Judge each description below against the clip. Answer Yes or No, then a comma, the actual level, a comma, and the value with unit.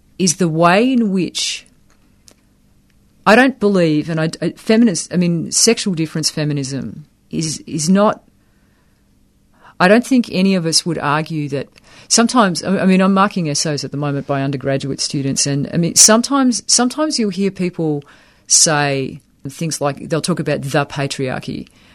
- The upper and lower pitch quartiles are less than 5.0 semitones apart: No, wide, 5.4 semitones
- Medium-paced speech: Yes, average, 155 wpm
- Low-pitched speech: No, medium, 165 Hz